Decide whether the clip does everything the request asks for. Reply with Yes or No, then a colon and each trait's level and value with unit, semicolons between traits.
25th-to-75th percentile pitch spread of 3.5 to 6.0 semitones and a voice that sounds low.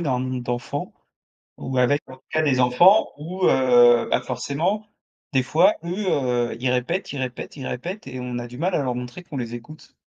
Yes: average, 4.2 semitones; low, 130 Hz